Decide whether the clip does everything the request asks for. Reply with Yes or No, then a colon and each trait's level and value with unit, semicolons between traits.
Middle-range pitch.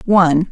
Yes: medium, 175 Hz